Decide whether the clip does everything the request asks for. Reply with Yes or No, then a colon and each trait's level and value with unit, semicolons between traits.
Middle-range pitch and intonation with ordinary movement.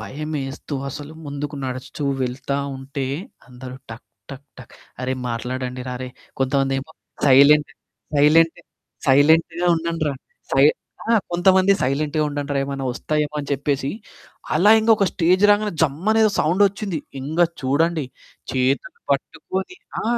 Yes: medium, 145 Hz; average, 3.5 semitones